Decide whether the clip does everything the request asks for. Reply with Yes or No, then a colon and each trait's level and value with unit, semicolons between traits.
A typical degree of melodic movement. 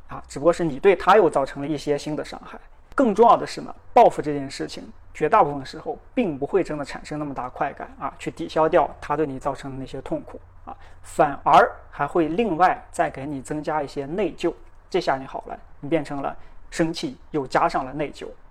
Yes: average, 3.1 semitones